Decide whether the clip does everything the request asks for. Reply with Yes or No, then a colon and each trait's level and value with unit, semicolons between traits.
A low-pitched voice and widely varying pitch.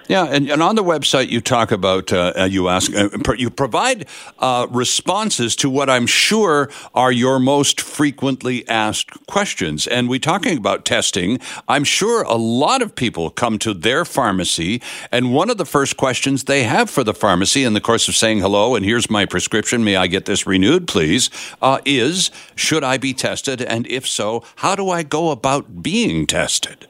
No: low, 125 Hz; average, 4.7 semitones